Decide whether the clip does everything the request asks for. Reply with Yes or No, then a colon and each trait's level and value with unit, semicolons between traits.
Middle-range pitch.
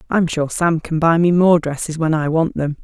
Yes: medium, 160 Hz